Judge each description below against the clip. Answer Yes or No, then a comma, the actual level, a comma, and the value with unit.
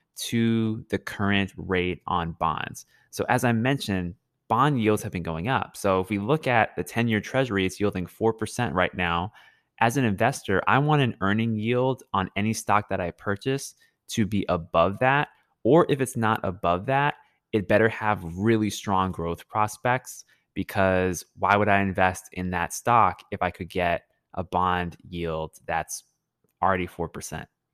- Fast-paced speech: No, average, 170 wpm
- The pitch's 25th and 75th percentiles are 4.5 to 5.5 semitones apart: No, average, 4.1 semitones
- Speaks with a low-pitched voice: Yes, low, 100 Hz